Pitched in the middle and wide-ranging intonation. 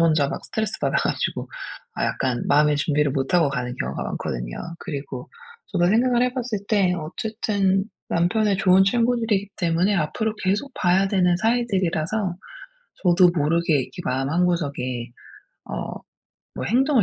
Yes: medium, 180 Hz; wide, 6.0 semitones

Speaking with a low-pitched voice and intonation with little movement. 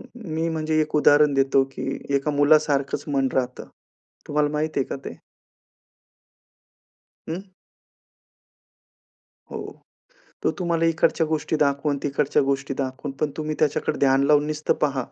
No: medium, 145 Hz; narrow, 2.1 semitones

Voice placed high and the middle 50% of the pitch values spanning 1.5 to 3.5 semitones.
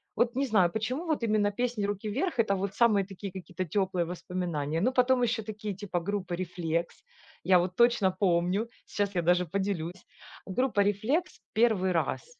No: high, 200 Hz; average, 3.9 semitones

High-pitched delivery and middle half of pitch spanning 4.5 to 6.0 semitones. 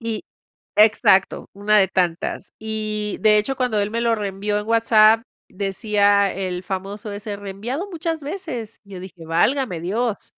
No: high, 210 Hz; narrow, 2.6 semitones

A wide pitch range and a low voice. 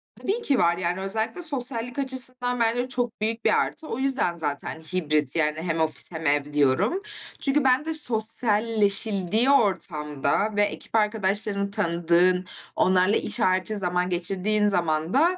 No: wide, 5.9 semitones; high, 205 Hz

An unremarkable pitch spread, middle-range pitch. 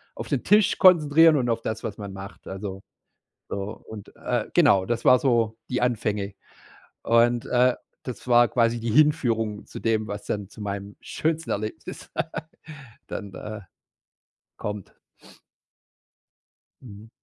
No: average, 3.2 semitones; low, 115 Hz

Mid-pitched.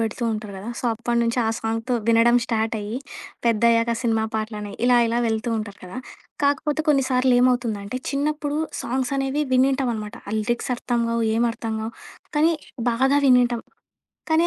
No: high, 235 Hz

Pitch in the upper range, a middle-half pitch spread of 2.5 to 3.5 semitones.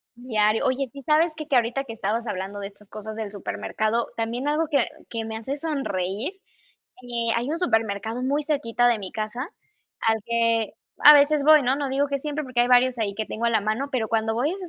No: high, 235 Hz; average, 4.2 semitones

